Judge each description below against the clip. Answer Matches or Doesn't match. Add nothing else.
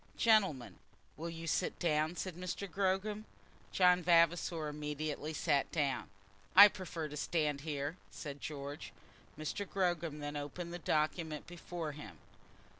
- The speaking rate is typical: Doesn't match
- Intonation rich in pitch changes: Doesn't match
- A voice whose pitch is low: Doesn't match